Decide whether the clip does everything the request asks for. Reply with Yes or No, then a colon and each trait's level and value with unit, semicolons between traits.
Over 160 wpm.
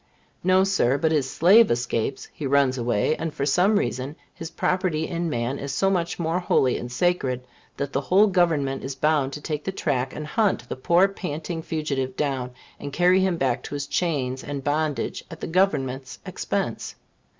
Yes: average, 185 wpm